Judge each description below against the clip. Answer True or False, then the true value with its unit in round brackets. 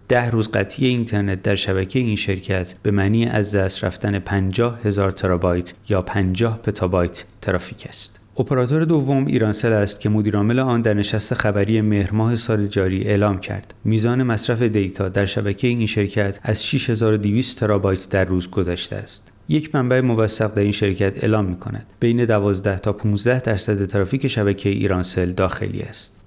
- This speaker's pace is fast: True (160 wpm)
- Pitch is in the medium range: False (105 Hz)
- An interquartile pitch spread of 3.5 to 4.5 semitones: False (2.8 semitones)